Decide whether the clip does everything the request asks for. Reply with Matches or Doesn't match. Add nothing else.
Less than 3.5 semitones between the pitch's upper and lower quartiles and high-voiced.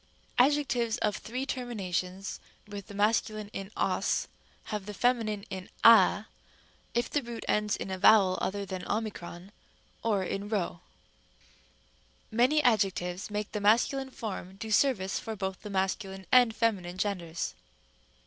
Matches